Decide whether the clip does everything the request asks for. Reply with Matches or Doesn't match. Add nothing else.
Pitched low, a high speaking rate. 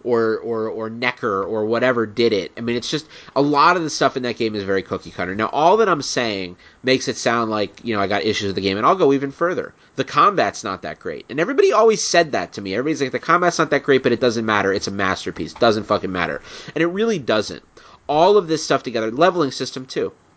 Matches